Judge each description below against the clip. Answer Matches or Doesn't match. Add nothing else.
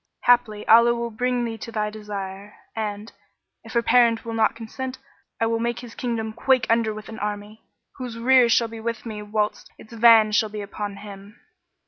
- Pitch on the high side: Matches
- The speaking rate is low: Doesn't match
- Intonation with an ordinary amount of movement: Doesn't match